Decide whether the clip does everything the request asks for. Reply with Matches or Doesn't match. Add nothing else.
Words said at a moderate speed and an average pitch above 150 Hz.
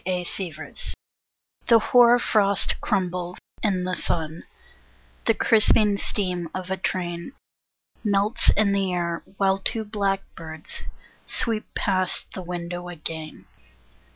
Doesn't match